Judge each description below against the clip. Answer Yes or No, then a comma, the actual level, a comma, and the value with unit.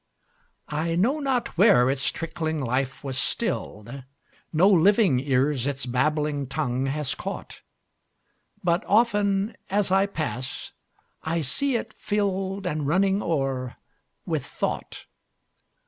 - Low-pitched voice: No, medium, 155 Hz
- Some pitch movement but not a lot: No, wide, 6.4 semitones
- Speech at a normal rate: No, slow, 105 wpm